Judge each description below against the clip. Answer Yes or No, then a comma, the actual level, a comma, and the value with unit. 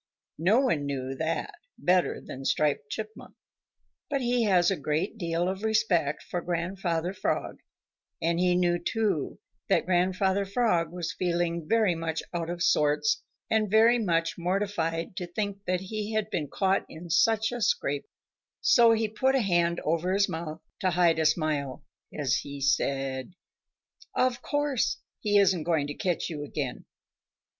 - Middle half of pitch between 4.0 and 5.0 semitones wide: Yes, average, 4.3 semitones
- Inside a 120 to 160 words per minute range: Yes, average, 155 wpm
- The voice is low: No, medium, 175 Hz